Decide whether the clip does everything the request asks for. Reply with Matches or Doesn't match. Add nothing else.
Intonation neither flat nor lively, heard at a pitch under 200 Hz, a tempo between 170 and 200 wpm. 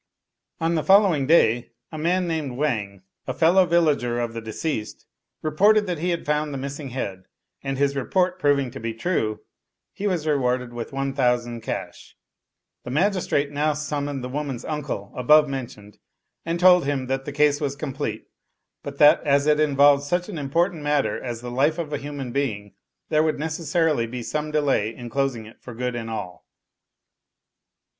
Matches